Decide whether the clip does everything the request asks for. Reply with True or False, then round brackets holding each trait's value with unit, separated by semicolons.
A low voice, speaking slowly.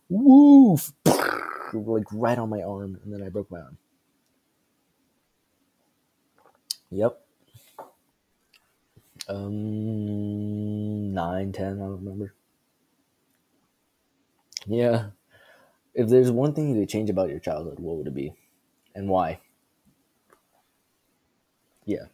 True (105 Hz; 100 wpm)